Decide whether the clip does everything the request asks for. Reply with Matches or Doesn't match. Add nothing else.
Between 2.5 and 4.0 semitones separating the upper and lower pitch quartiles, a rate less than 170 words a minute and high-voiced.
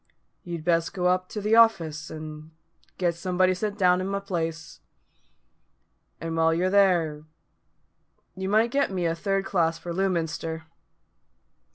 Doesn't match